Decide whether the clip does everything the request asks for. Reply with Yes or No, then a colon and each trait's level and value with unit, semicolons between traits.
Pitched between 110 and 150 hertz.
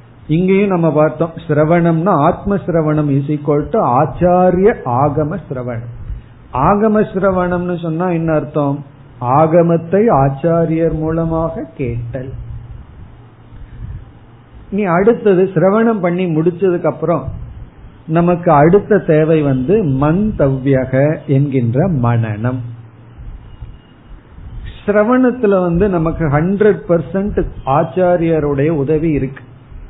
No: medium, 160 Hz